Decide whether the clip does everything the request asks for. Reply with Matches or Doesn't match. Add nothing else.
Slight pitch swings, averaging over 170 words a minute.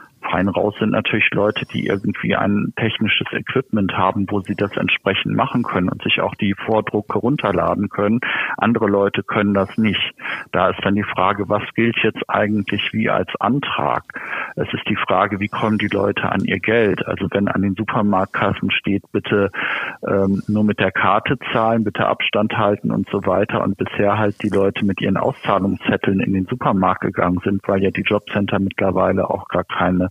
Matches